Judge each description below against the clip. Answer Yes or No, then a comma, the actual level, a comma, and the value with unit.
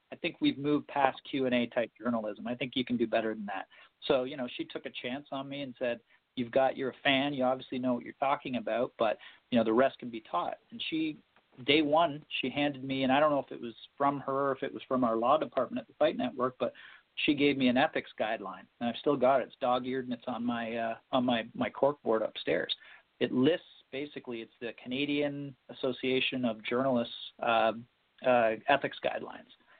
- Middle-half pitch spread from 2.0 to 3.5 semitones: Yes, narrow, 2.6 semitones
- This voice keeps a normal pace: No, fast, 230 wpm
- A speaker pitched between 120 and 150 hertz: Yes, low, 130 Hz